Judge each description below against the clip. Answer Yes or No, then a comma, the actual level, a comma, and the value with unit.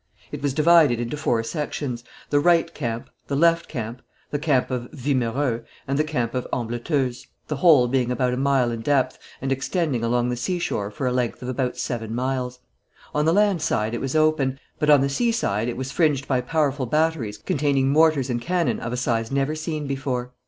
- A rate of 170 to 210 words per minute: Yes, average, 200 wpm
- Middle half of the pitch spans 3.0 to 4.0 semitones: Yes, average, 3.7 semitones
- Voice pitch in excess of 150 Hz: No, low, 135 Hz